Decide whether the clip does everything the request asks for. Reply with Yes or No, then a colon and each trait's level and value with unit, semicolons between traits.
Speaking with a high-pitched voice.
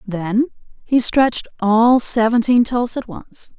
Yes: high, 230 Hz